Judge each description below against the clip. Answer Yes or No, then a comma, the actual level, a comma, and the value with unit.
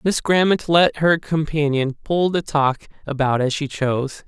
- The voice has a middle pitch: Yes, medium, 150 Hz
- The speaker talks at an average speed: Yes, average, 170 wpm